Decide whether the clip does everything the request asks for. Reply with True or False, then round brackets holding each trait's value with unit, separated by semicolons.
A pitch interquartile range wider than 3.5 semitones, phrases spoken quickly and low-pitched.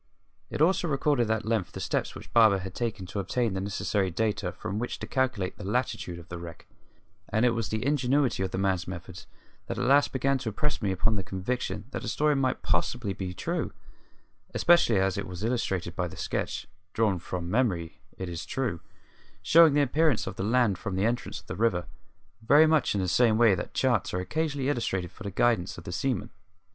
True (5.2 semitones; 210 wpm; 110 Hz)